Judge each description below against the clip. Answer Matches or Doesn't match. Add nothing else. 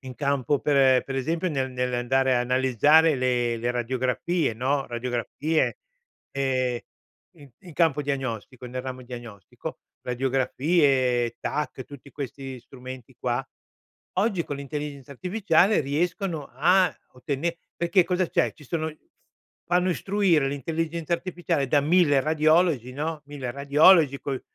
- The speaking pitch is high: Doesn't match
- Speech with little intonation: Doesn't match